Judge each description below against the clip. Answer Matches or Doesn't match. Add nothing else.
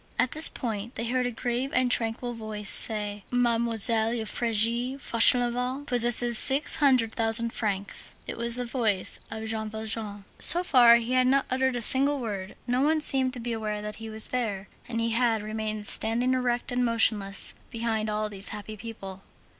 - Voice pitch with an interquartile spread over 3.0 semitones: Doesn't match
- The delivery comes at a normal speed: Matches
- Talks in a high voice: Matches